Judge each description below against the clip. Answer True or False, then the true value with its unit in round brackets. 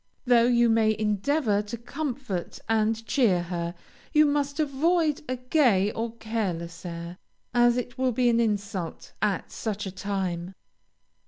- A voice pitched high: True (225 Hz)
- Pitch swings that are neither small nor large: True (4.5 semitones)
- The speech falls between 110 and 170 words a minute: True (145 wpm)